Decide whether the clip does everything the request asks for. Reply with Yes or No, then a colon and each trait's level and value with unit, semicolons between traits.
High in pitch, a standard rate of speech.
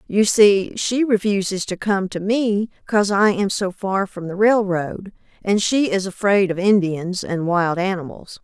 Yes: high, 195 Hz; average, 180 wpm